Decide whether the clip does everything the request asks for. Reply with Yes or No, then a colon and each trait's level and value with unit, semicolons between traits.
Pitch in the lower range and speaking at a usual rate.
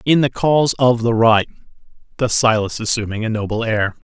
Yes: low, 115 Hz; average, 175 wpm